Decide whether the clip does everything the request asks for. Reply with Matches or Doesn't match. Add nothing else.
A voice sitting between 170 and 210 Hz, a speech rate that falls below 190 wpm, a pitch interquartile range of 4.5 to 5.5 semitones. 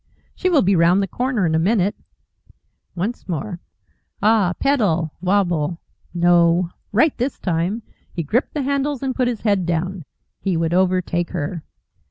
Matches